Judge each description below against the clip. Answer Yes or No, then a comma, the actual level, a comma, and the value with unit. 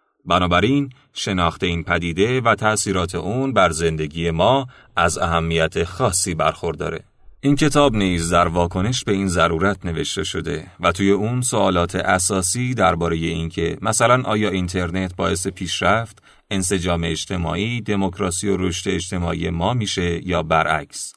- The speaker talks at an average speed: Yes, average, 130 wpm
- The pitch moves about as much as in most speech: Yes, average, 3.7 semitones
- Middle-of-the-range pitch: No, very low, 95 Hz